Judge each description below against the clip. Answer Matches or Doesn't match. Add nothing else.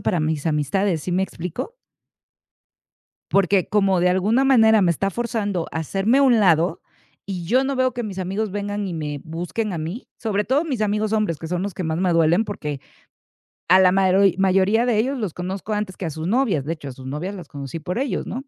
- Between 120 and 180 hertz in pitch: Doesn't match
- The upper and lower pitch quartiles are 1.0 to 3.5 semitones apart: Doesn't match